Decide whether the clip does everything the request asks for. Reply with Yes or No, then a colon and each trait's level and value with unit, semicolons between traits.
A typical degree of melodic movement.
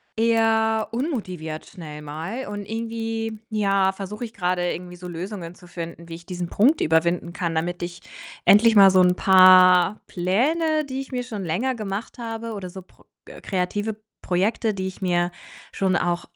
Yes: average, 4.1 semitones